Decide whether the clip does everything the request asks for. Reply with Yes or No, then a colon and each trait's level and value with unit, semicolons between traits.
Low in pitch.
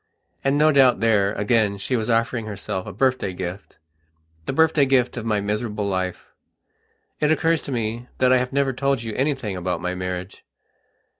Yes: low, 115 Hz